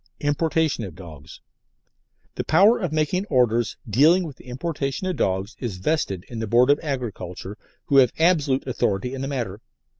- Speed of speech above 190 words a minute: No, average, 170 wpm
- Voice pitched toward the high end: No, low, 130 Hz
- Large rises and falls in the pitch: Yes, wide, 6.6 semitones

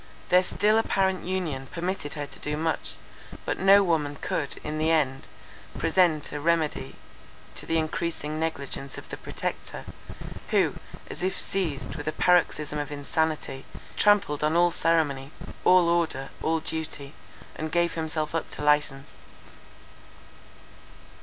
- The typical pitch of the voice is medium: Yes, medium, 160 Hz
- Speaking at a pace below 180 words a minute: Yes, average, 140 wpm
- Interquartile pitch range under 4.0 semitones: Yes, average, 2.8 semitones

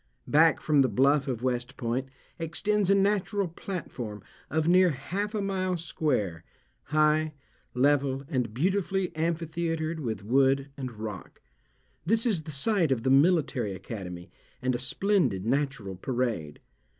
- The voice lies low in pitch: No, medium, 145 Hz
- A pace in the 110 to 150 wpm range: Yes, average, 140 wpm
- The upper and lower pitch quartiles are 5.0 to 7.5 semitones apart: Yes, wide, 5.5 semitones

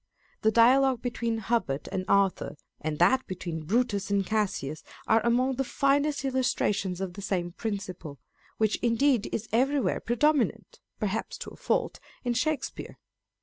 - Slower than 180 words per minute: Yes, average, 145 wpm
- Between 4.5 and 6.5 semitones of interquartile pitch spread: Yes, average, 5.1 semitones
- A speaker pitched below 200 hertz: No, high, 225 Hz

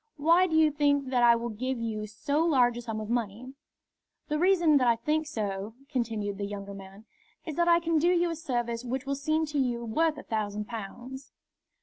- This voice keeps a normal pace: No, fast, 215 wpm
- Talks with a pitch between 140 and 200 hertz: No, very high, 255 Hz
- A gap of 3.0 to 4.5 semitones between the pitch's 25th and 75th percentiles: No, wide, 5.6 semitones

